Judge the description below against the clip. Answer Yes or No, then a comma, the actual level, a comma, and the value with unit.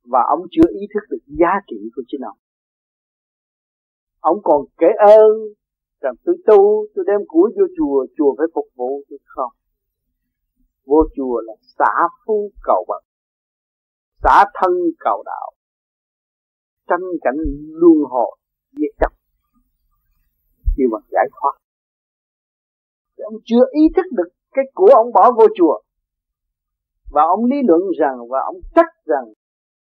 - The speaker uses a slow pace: Yes, slow, 140 wpm